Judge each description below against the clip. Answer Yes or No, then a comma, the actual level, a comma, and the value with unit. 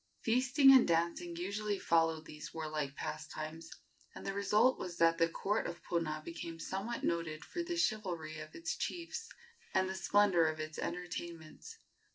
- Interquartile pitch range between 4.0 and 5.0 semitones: Yes, average, 4.7 semitones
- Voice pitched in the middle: Yes, medium, 170 Hz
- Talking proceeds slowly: No, average, 160 wpm